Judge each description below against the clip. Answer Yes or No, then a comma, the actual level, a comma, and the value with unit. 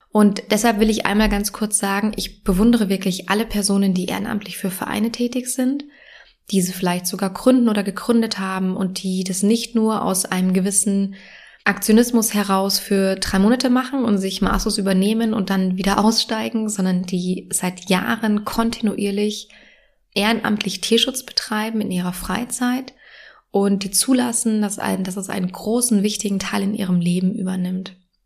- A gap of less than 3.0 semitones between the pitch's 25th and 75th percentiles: Yes, narrow, 2.5 semitones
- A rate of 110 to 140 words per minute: No, average, 160 wpm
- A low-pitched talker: No, high, 205 Hz